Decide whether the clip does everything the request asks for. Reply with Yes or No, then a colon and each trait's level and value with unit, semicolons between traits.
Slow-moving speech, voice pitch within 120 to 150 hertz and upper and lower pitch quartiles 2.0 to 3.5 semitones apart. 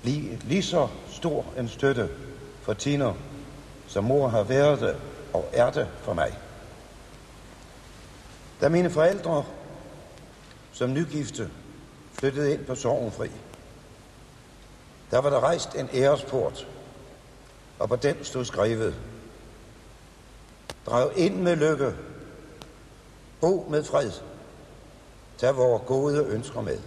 Yes: slow, 110 wpm; low, 135 Hz; average, 2.8 semitones